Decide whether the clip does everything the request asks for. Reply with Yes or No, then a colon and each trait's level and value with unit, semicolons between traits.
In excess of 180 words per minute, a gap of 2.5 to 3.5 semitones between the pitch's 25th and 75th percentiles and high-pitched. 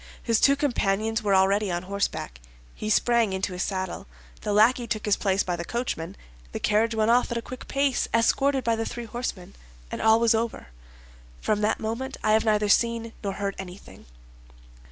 Yes: average, 190 wpm; average, 2.9 semitones; high, 220 Hz